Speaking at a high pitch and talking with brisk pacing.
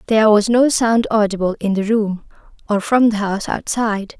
No: high, 215 Hz; average, 185 wpm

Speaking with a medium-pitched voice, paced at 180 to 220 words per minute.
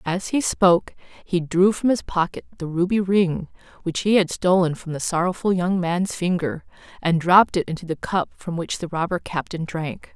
Yes: medium, 175 Hz; average, 195 wpm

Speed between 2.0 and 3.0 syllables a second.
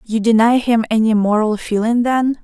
No: 4.9 syllables/s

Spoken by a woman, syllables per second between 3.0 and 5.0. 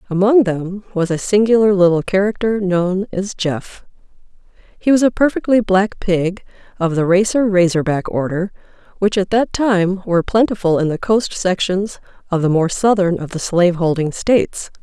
Yes: female; 4.9 syllables/s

